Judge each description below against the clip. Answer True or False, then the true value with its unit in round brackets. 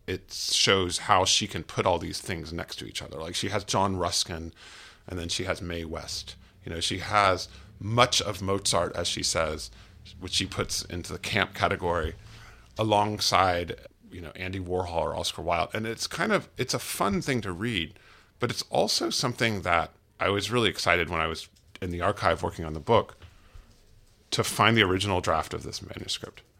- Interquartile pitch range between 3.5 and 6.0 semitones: False (3.1 semitones)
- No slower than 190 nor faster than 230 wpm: True (195 wpm)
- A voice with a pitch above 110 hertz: False (95 Hz)